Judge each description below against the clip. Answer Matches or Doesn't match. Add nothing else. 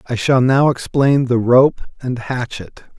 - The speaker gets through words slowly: Doesn't match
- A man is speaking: Matches